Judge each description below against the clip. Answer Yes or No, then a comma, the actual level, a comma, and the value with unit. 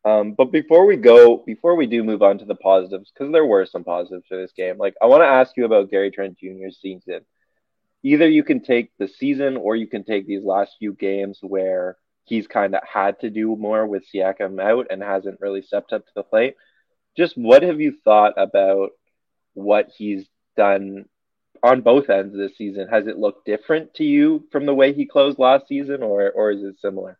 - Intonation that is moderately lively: No, wide, 6.1 semitones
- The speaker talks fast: Yes, fast, 215 wpm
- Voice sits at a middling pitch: No, low, 105 Hz